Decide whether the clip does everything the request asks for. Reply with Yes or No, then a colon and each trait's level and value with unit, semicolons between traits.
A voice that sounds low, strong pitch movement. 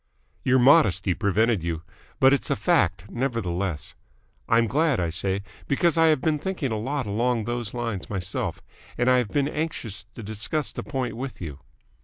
Yes: low, 120 Hz; wide, 5.7 semitones